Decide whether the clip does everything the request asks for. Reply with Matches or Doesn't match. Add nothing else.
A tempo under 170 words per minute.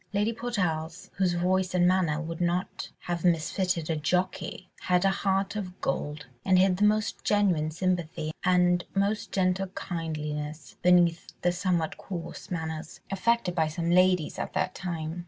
Matches